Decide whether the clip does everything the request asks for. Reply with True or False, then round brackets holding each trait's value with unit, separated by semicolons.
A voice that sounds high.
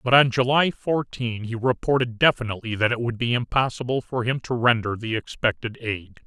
False (120 Hz)